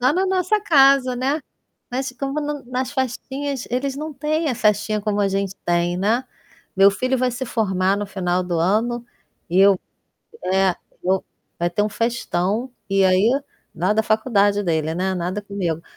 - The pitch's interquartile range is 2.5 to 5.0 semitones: No, wide, 5.6 semitones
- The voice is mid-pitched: No, high, 215 Hz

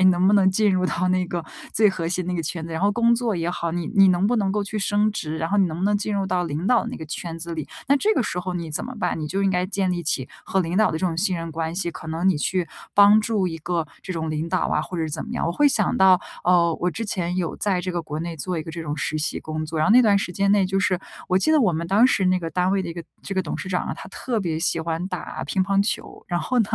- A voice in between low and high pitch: Yes, medium, 180 Hz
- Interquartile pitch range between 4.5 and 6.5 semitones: No, average, 3.1 semitones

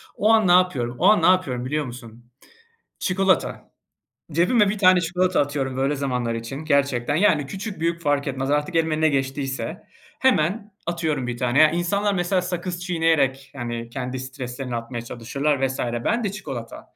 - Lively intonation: Yes, wide, 5.7 semitones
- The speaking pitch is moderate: Yes, medium, 145 Hz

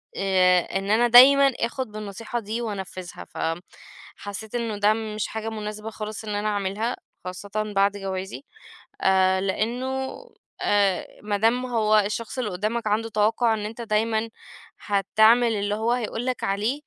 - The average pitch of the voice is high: Yes, high, 215 Hz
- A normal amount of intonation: No, narrow, 2.1 semitones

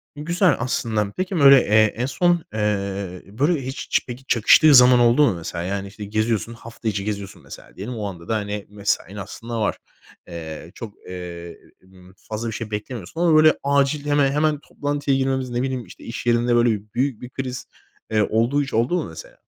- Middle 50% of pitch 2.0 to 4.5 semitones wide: No, average, 5.2 semitones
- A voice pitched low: Yes, low, 115 Hz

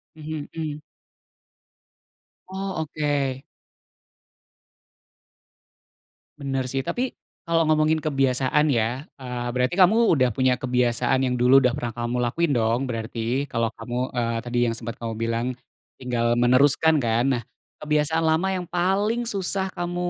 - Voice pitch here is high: No, low, 135 Hz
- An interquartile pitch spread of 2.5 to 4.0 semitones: No, average, 4.6 semitones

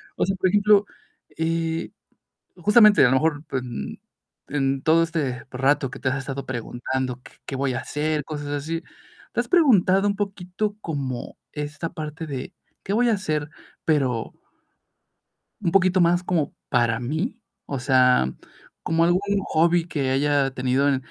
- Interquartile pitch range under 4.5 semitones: No, average, 4.9 semitones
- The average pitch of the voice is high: No, medium, 150 Hz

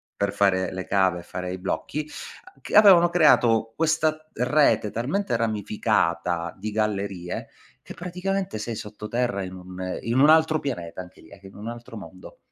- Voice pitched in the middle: No, low, 110 Hz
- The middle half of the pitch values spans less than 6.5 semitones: No, wide, 8.3 semitones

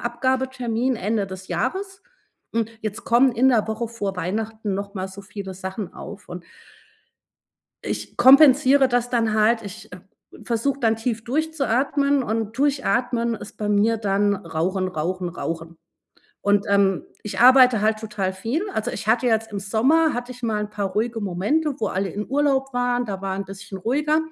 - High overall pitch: Yes, high, 220 Hz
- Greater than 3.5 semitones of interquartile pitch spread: Yes, average, 4.2 semitones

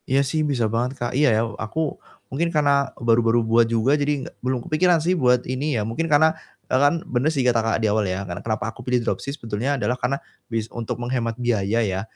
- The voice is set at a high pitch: No, low, 125 Hz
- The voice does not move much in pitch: No, average, 3.7 semitones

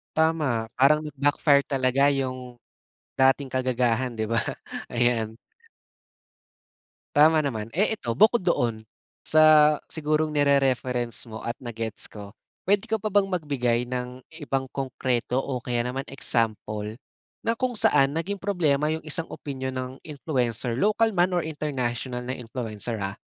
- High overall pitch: No, low, 130 Hz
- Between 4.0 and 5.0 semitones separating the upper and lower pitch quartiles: Yes, average, 4.3 semitones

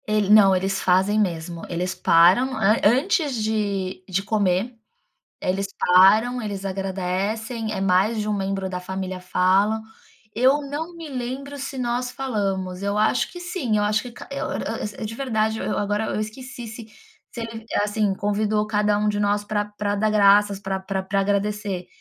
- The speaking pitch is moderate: No, high, 210 Hz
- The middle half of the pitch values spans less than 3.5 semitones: Yes, average, 2.8 semitones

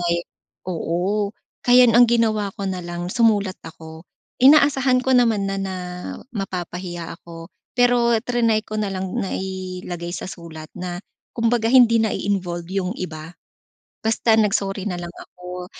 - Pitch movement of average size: Yes, average, 4.5 semitones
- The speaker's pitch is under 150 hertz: No, high, 195 Hz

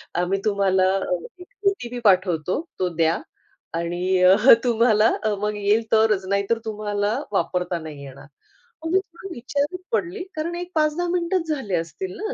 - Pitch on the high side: Yes, high, 215 Hz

